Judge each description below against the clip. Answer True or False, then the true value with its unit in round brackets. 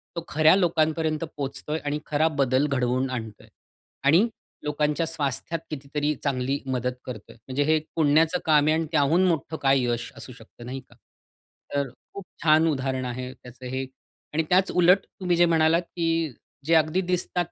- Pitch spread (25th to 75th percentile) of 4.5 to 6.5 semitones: False (3.8 semitones)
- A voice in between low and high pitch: True (150 Hz)